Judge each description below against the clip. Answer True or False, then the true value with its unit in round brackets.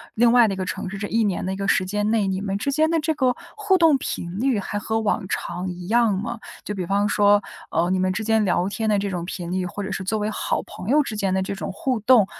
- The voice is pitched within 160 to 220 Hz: True (205 Hz)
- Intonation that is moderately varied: True (3.4 semitones)